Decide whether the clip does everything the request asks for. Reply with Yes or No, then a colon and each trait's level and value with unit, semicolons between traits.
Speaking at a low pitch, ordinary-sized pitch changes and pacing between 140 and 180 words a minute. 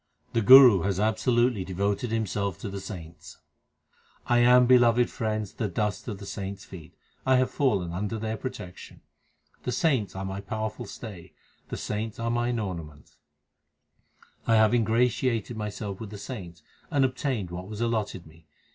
Yes: low, 110 Hz; average, 3.7 semitones; average, 155 wpm